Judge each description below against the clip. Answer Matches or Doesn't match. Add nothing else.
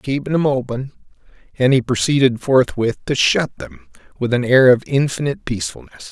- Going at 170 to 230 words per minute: Doesn't match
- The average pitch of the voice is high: Doesn't match